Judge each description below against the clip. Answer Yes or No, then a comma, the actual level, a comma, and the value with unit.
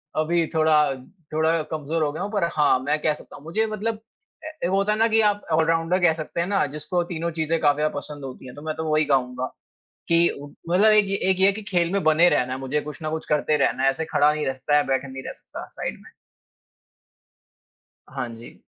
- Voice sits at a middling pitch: Yes, medium, 160 Hz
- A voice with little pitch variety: No, average, 3.3 semitones